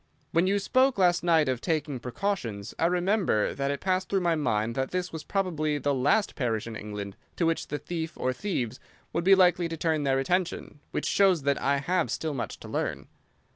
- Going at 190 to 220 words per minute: Yes, fast, 205 wpm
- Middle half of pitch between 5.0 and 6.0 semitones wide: Yes, wide, 5.4 semitones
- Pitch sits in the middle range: Yes, medium, 160 Hz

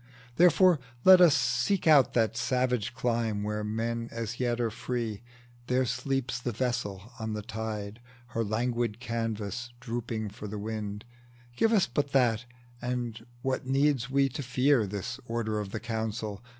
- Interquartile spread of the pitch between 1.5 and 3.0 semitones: Yes, narrow, 2.5 semitones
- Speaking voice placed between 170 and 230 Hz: No, low, 115 Hz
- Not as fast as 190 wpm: Yes, average, 155 wpm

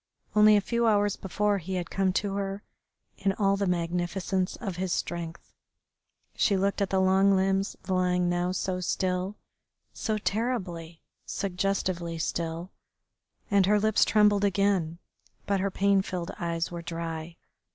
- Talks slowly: No, average, 145 wpm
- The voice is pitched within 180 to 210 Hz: Yes, high, 190 Hz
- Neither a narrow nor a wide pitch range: No, narrow, 2.3 semitones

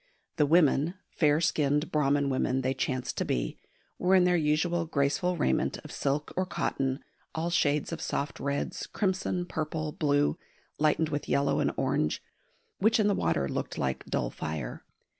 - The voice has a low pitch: No, medium, 150 Hz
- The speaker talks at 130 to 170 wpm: Yes, average, 160 wpm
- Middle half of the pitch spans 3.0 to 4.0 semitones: Yes, average, 3.7 semitones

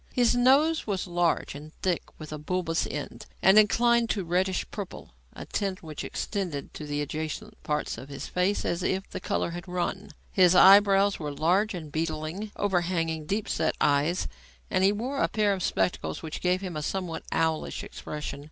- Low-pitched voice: No, medium, 180 Hz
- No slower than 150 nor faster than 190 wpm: Yes, average, 185 wpm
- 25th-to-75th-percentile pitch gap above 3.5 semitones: Yes, average, 4.2 semitones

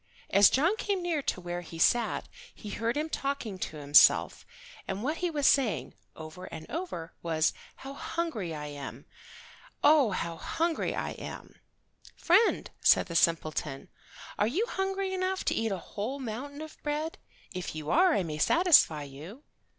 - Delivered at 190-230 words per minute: No, average, 165 wpm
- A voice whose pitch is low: No, high, 230 Hz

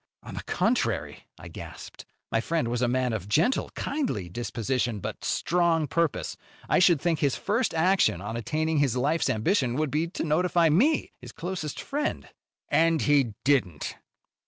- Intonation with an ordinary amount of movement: No, wide, 5.9 semitones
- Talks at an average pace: Yes, average, 160 wpm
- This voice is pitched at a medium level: Yes, medium, 150 Hz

